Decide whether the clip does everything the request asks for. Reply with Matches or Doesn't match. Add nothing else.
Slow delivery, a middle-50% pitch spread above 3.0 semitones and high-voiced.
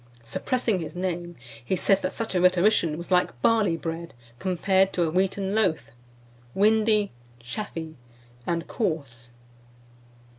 Doesn't match